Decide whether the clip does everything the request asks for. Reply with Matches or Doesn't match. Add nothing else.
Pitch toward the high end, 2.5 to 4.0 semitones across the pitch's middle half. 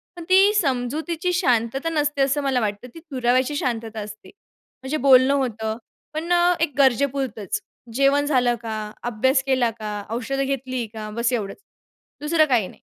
Matches